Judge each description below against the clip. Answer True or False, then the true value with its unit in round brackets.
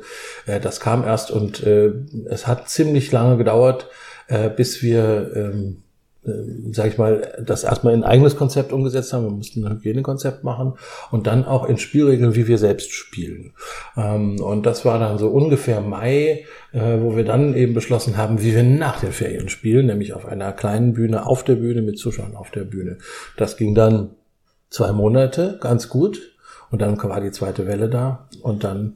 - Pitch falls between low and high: False (115 Hz)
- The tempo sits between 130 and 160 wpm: False (185 wpm)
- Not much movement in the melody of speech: False (3.3 semitones)